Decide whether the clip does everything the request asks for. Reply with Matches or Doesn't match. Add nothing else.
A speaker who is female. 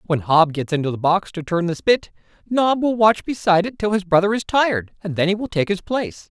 Doesn't match